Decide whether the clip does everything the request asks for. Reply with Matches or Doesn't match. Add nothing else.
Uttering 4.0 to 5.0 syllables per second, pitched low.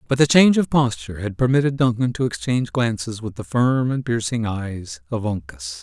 Doesn't match